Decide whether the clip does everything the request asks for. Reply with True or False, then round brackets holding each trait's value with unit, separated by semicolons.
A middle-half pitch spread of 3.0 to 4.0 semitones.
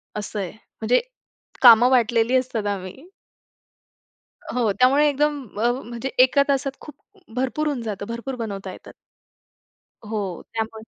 True (3.5 semitones)